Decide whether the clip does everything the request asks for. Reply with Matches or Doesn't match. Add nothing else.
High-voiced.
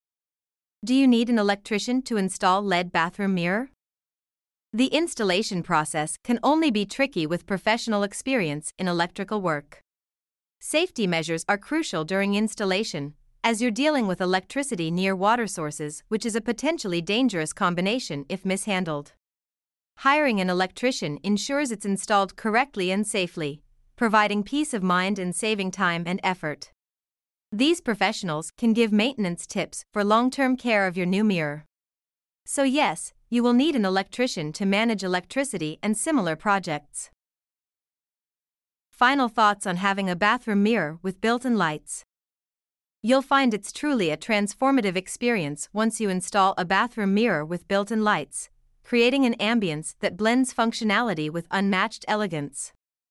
Matches